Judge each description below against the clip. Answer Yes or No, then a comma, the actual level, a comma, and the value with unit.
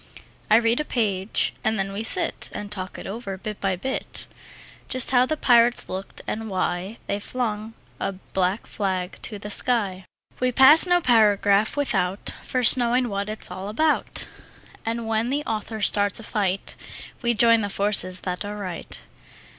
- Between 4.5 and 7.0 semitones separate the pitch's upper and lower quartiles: No, average, 3.3 semitones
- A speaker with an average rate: Yes, average, 170 wpm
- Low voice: No, high, 215 Hz